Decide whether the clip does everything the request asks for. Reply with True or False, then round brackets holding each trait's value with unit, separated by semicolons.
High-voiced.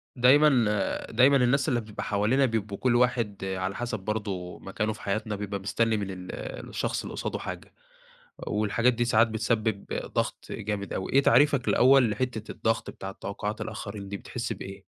False (110 Hz)